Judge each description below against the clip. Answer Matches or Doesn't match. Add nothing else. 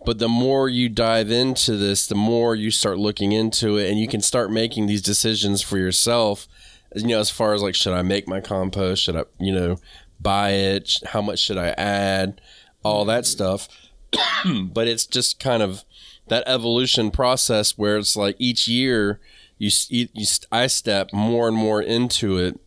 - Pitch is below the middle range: Matches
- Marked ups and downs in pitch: Doesn't match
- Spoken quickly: Doesn't match